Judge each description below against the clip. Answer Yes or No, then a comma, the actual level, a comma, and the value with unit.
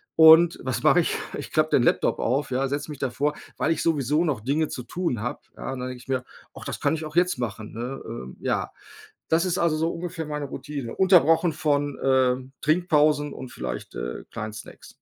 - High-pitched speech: No, medium, 145 Hz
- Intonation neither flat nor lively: Yes, average, 4.1 semitones